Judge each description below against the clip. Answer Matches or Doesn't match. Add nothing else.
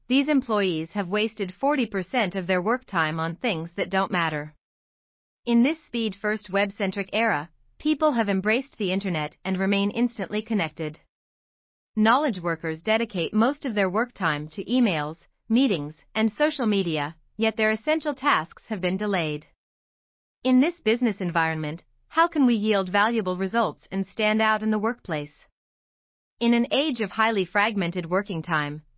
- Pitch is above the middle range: Matches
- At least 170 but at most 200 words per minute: Doesn't match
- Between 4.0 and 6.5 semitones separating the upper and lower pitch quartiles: Matches